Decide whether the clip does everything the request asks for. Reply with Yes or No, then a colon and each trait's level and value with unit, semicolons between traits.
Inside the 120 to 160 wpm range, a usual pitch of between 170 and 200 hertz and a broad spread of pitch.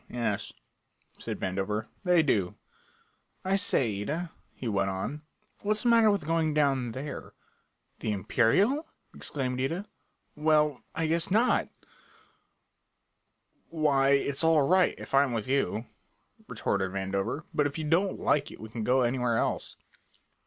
No: average, 140 wpm; medium, 140 Hz; wide, 6.2 semitones